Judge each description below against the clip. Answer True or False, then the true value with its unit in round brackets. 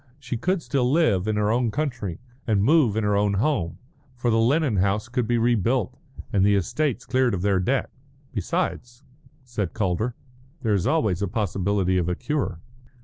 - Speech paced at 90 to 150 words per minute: False (180 wpm)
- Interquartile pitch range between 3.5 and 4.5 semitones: True (4.1 semitones)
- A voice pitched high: False (110 Hz)